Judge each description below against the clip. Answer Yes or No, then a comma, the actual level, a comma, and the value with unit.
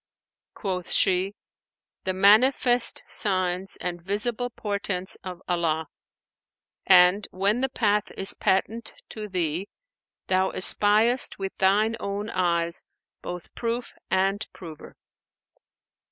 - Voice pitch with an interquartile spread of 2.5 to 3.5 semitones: Yes, average, 2.8 semitones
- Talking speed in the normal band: No, slow, 105 wpm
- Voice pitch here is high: Yes, high, 195 Hz